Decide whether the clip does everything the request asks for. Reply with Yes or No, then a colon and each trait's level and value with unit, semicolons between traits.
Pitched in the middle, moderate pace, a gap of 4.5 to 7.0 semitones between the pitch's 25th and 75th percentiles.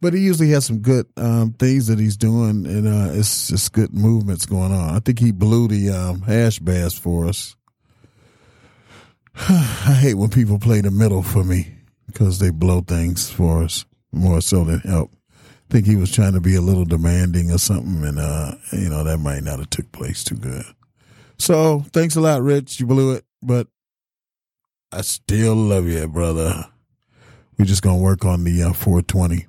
No: low, 105 Hz; average, 195 wpm; average, 4.8 semitones